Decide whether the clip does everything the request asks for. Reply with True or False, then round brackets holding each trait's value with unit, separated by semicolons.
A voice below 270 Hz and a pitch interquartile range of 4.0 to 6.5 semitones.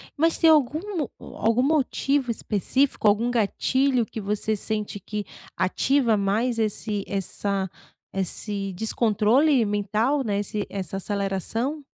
True (220 Hz; 4.6 semitones)